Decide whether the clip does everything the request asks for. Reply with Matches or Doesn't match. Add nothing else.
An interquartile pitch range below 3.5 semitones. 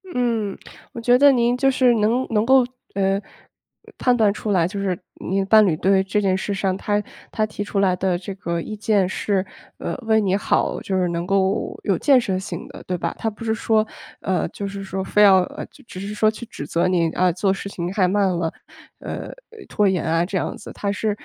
Matches